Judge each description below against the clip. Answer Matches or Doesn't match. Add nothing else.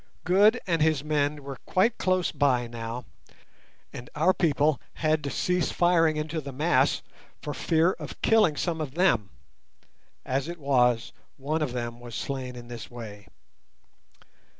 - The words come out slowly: Doesn't match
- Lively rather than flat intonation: Doesn't match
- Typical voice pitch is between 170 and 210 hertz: Doesn't match